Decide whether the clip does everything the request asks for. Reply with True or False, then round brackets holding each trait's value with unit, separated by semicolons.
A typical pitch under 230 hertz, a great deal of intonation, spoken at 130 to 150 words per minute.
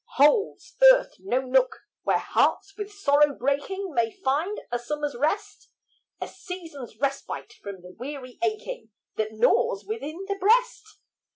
False (295 Hz; 8.0 semitones; 135 wpm)